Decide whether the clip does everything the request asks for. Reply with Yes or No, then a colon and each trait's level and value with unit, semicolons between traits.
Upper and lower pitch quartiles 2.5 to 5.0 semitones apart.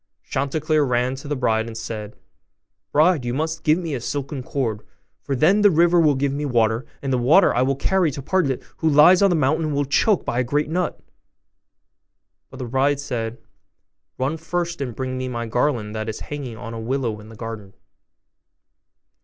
Yes: average, 4.4 semitones